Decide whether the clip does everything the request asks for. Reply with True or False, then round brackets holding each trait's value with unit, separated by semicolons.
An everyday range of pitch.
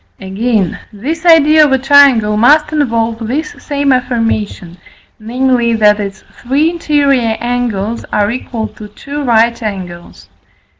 True (4.8 semitones)